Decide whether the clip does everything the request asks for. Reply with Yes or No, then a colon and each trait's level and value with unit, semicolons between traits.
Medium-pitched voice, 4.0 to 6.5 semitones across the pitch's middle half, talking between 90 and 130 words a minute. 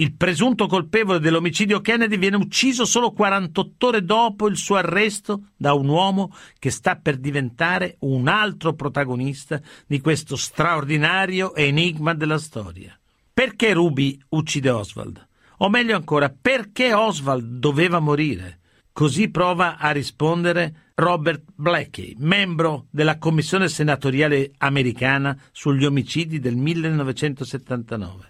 Yes: medium, 160 Hz; average, 5.2 semitones; average, 120 wpm